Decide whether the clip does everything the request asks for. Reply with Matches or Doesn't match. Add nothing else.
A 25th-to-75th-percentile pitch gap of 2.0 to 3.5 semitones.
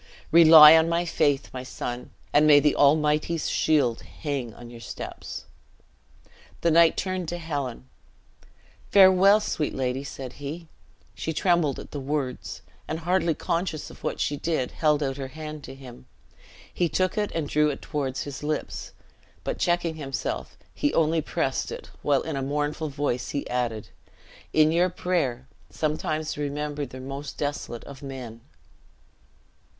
Matches